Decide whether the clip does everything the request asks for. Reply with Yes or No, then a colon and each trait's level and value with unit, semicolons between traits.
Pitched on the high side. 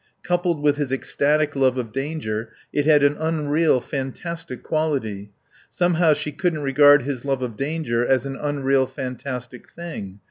No: medium, 140 Hz